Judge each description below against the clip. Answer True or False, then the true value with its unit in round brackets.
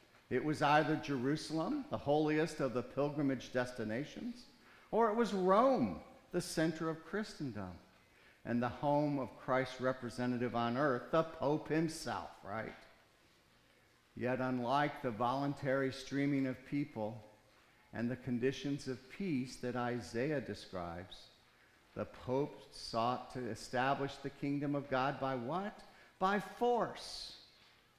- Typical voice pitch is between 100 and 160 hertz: True (140 Hz)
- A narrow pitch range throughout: False (4.2 semitones)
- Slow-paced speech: True (125 wpm)